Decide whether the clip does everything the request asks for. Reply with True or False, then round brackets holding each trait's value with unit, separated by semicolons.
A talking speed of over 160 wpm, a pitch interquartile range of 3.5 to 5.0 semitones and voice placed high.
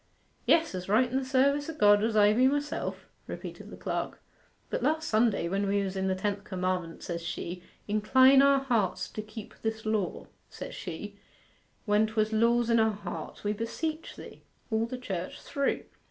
True (185 wpm; 4.4 semitones; 215 Hz)